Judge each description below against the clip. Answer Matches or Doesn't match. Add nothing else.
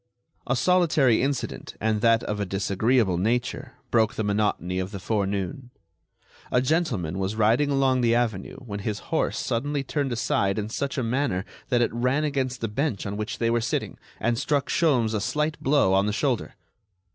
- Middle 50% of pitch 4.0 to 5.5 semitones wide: Matches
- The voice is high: Doesn't match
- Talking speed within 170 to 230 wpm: Matches